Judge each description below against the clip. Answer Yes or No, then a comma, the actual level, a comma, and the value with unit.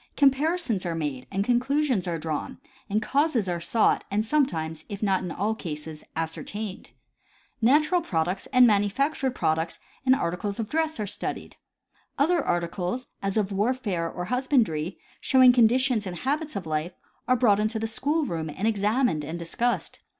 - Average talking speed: Yes, average, 165 wpm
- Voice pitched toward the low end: No, high, 210 Hz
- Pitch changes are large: Yes, wide, 6.8 semitones